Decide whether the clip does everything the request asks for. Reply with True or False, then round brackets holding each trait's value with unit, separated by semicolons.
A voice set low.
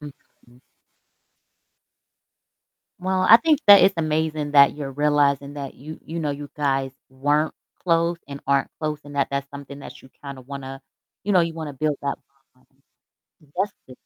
False (145 Hz)